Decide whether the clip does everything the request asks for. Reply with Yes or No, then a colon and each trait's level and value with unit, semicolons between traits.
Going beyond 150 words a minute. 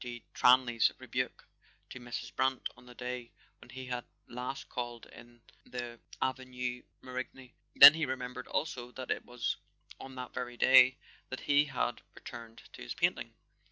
Yes: average, 160 wpm